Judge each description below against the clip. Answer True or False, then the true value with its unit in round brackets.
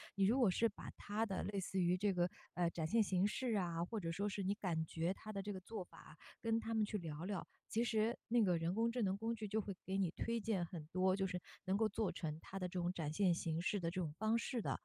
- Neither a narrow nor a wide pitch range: True (3.6 semitones)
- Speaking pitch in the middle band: False (195 Hz)